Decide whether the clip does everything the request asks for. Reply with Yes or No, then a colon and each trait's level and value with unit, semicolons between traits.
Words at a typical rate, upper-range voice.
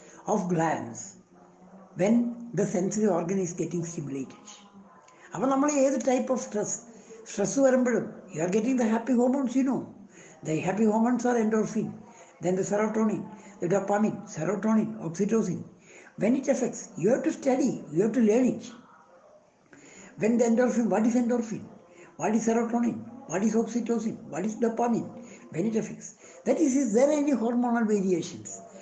No: fast, 150 wpm; high, 220 Hz